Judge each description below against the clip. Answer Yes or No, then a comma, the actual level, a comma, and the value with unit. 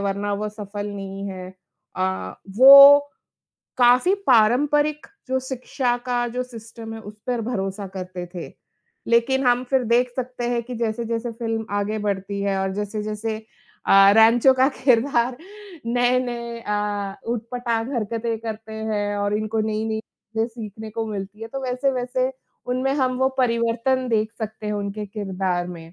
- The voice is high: Yes, high, 225 Hz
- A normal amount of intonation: Yes, average, 3.1 semitones